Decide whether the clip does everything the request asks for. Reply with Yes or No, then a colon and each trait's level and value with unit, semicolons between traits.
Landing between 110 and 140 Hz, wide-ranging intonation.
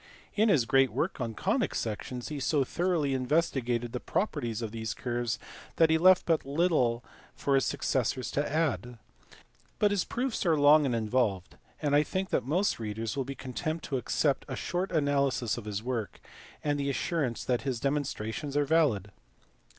No: low, 135 Hz; average, 4.7 semitones